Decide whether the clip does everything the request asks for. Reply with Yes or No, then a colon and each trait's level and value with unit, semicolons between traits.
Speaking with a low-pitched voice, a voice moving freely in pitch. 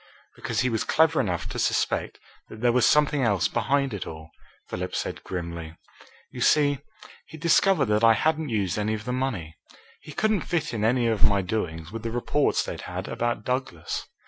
Yes: low, 115 Hz; wide, 6.2 semitones